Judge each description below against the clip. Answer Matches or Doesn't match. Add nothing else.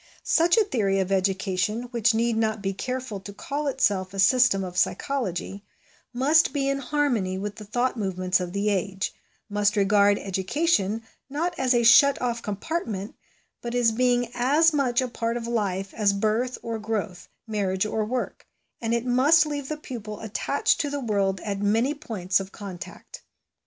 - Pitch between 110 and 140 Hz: Doesn't match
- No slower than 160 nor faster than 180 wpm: Matches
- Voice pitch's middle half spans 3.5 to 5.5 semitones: Matches